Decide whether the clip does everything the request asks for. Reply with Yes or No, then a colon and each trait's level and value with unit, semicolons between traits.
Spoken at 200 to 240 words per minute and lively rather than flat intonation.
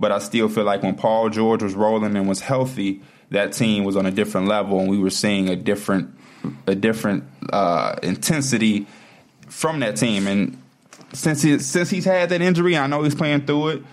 Yes: fast, 205 wpm; wide, 6.6 semitones